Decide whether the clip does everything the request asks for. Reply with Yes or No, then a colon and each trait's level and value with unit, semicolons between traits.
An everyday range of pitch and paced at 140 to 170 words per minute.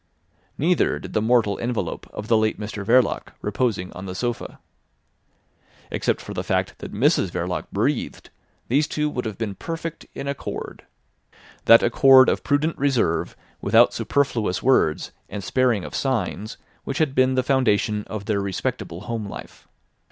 Yes: average, 4.2 semitones; average, 155 wpm